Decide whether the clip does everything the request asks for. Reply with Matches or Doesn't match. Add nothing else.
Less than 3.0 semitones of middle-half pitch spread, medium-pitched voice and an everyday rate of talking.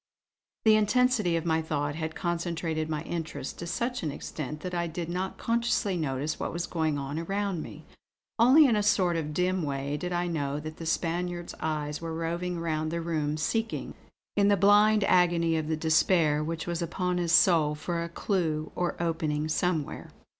Matches